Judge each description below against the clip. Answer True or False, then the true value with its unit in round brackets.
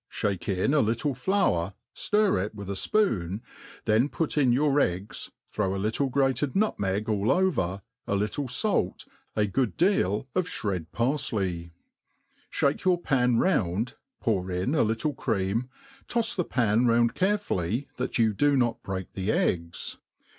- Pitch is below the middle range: True (115 Hz)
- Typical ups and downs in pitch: False (6.6 semitones)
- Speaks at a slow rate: False (145 wpm)